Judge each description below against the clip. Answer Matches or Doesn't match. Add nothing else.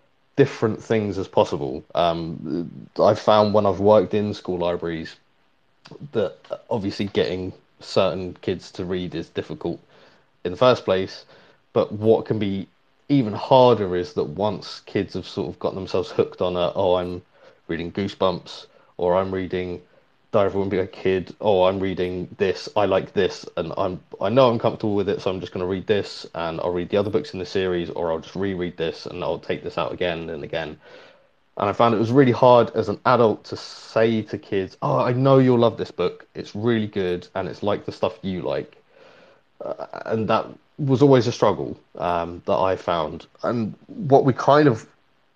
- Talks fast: Doesn't match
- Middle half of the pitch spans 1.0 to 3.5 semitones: Doesn't match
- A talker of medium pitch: Doesn't match